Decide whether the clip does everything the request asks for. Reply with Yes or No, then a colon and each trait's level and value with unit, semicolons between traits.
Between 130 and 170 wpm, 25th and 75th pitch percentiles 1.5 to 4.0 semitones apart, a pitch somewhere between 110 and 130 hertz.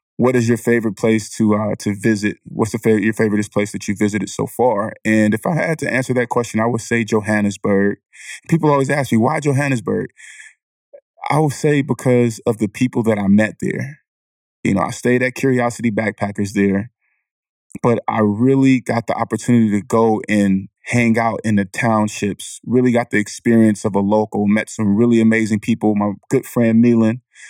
No: average, 190 wpm; average, 2.8 semitones; low, 115 Hz